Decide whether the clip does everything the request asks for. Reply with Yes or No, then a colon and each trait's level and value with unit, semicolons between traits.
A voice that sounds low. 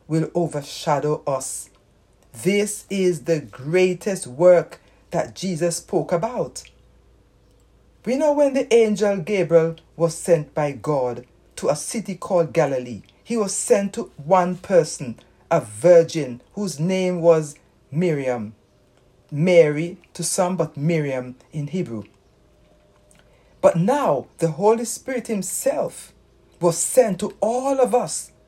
No: medium, 170 Hz